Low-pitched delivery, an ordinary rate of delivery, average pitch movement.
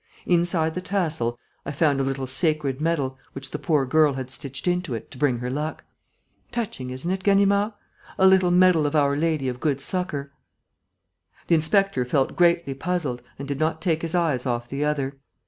No: medium, 150 Hz; average, 185 wpm; average, 4.5 semitones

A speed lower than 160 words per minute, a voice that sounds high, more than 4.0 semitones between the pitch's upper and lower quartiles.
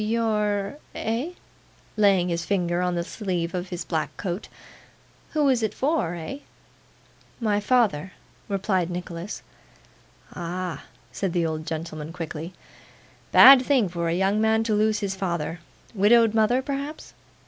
Yes: slow, 135 wpm; high, 195 Hz; average, 4.4 semitones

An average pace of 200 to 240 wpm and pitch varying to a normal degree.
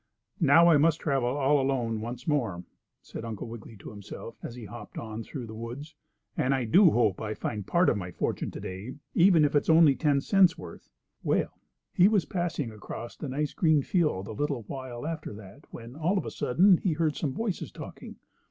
No: fast, 205 wpm; wide, 5.9 semitones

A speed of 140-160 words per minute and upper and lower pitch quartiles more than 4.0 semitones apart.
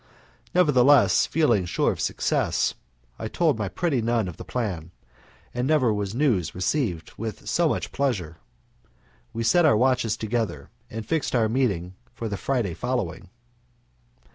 Yes: average, 145 wpm; average, 5.2 semitones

